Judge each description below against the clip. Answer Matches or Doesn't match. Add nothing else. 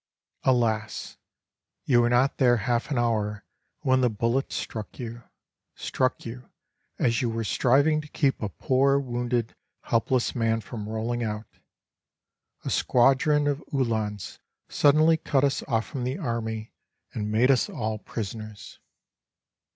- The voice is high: Doesn't match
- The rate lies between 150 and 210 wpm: Doesn't match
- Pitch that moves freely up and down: Doesn't match